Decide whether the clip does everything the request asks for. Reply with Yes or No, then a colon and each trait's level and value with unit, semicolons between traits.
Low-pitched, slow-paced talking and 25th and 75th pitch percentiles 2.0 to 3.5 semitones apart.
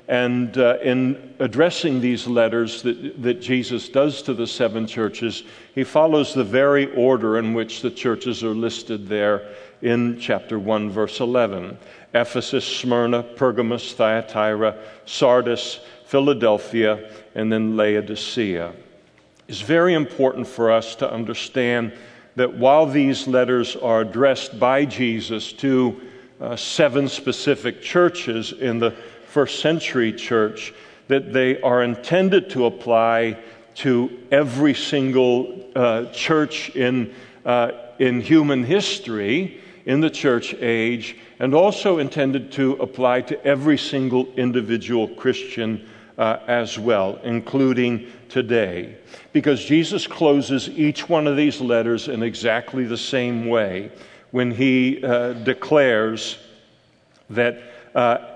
Yes: low, 125 Hz; slow, 120 wpm; average, 2.8 semitones